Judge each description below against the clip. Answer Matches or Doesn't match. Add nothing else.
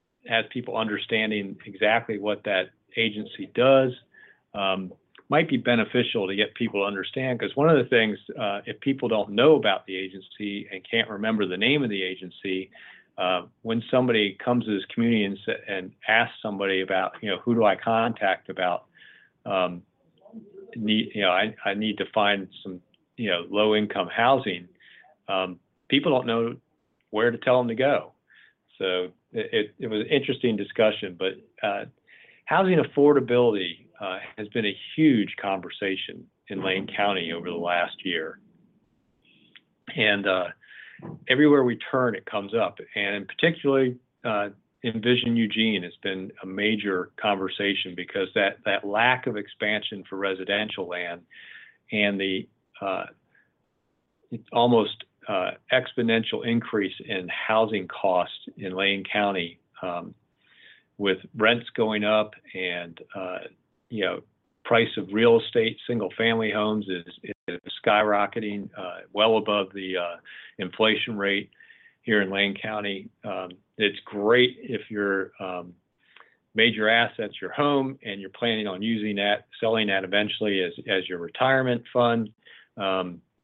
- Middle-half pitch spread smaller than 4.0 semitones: Matches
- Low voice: Matches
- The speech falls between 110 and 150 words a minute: Matches